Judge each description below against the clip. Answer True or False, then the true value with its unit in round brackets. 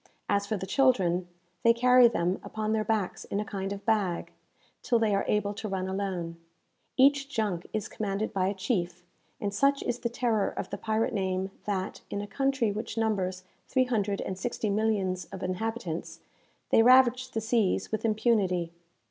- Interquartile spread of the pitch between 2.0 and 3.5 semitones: True (3.2 semitones)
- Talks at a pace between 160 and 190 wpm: True (180 wpm)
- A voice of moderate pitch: False (210 Hz)